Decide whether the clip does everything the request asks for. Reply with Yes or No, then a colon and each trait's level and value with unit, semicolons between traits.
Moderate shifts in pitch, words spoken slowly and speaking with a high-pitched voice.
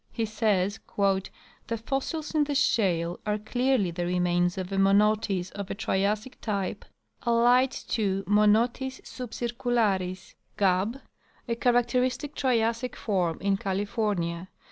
Yes: average, 4.2 semitones; slow, 125 wpm; high, 210 Hz